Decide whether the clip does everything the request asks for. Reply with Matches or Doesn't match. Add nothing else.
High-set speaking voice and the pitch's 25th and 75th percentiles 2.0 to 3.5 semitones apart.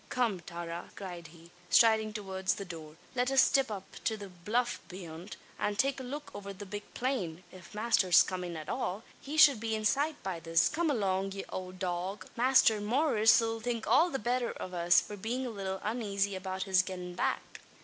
Doesn't match